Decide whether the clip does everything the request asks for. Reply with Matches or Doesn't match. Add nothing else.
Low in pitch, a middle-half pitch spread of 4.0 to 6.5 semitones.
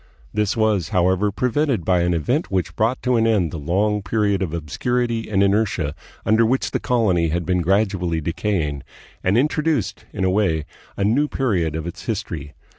Matches